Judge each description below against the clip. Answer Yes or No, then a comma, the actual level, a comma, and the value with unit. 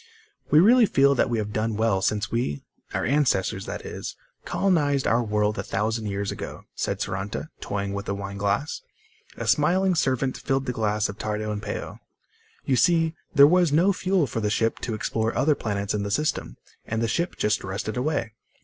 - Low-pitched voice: Yes, low, 115 Hz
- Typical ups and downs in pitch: No, wide, 5.9 semitones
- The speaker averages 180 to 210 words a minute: Yes, average, 190 wpm